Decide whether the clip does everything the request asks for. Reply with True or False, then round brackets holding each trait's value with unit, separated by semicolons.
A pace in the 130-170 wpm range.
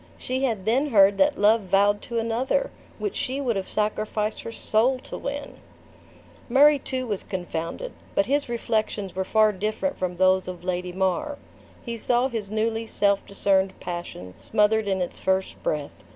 True (165 wpm)